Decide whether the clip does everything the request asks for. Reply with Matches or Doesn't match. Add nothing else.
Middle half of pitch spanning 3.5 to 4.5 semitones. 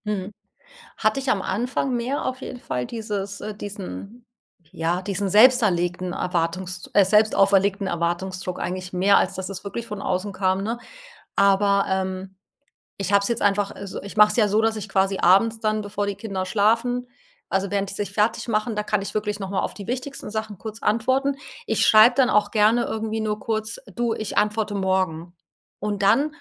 Doesn't match